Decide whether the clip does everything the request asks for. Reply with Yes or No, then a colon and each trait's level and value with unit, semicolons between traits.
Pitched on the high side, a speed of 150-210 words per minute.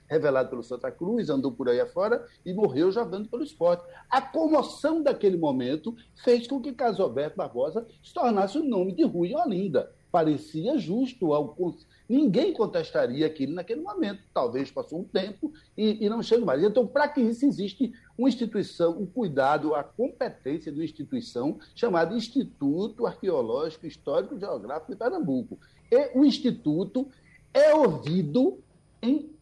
Yes: high, 235 Hz; average, 155 wpm